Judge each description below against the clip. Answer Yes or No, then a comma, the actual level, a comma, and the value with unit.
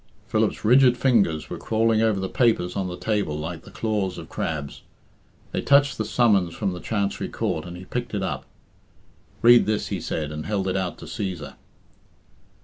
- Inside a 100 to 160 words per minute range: No, average, 185 wpm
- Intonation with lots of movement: No, average, 4.3 semitones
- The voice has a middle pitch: No, low, 100 Hz